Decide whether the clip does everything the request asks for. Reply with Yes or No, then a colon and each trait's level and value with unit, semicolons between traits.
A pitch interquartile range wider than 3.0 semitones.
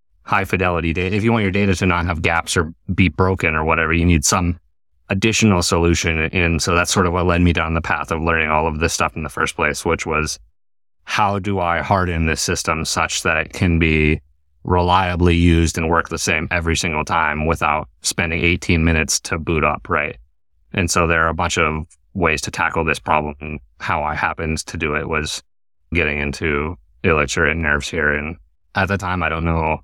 No: narrow, 2.5 semitones